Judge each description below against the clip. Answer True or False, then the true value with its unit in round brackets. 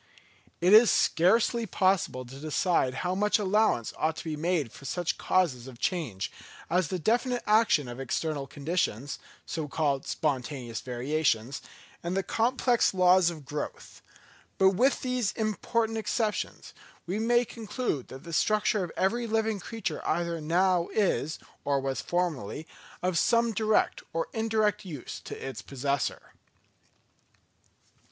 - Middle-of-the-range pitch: True (175 Hz)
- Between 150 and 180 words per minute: False (140 wpm)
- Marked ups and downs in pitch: True (7.1 semitones)